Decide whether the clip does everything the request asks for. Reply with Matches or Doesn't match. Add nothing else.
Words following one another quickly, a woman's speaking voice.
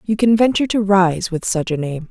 Matches